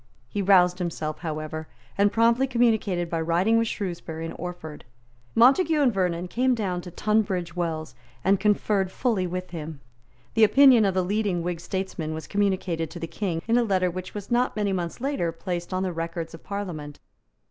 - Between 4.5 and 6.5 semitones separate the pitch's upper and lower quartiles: No, average, 3.9 semitones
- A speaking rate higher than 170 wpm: Yes, average, 180 wpm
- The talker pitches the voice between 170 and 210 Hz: Yes, medium, 185 Hz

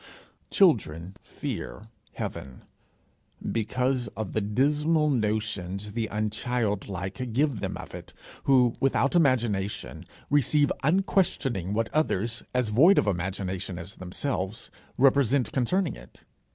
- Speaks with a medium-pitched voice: No, low, 115 Hz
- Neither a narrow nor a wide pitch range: No, wide, 5.7 semitones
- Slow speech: Yes, slow, 110 wpm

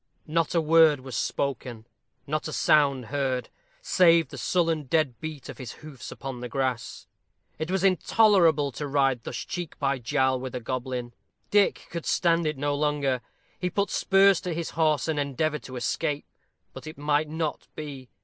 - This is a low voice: No, medium, 150 Hz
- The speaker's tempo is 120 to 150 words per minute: No, average, 175 wpm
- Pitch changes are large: No, average, 3.7 semitones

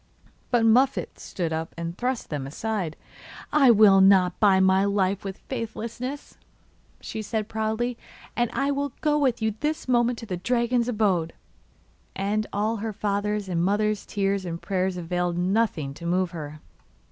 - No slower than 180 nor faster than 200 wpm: No, average, 160 wpm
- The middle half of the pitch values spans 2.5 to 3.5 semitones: No, average, 4.1 semitones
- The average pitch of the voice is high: Yes, high, 205 Hz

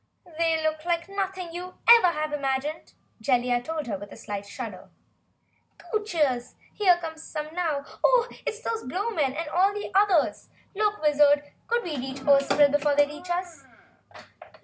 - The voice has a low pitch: No, very high, 320 Hz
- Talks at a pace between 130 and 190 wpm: Yes, average, 165 wpm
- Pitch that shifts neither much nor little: Yes, average, 4.3 semitones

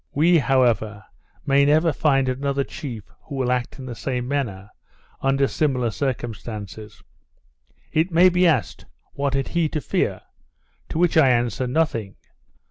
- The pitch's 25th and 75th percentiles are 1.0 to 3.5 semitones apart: No, average, 3.9 semitones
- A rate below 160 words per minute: Yes, average, 145 wpm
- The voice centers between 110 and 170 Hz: Yes, low, 135 Hz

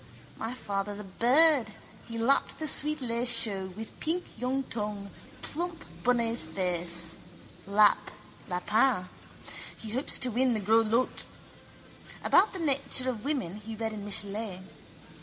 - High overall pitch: Yes, high, 225 Hz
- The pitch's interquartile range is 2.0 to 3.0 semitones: No, average, 4.2 semitones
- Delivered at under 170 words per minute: Yes, average, 140 wpm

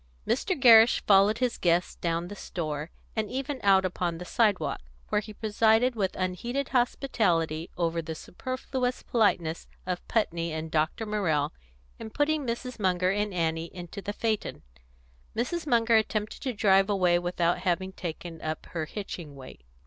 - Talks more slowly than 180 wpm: Yes, average, 155 wpm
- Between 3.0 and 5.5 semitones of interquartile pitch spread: Yes, average, 5.1 semitones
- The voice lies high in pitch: Yes, high, 195 Hz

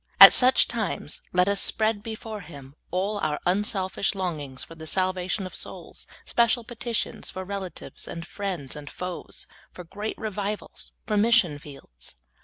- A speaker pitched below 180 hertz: No, high, 190 Hz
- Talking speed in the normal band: Yes, average, 150 wpm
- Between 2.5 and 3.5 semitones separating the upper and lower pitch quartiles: No, average, 4.3 semitones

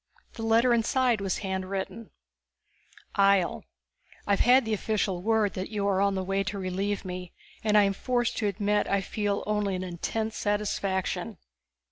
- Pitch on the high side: Yes, high, 200 Hz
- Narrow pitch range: Yes, narrow, 2.3 semitones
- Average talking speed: Yes, average, 160 wpm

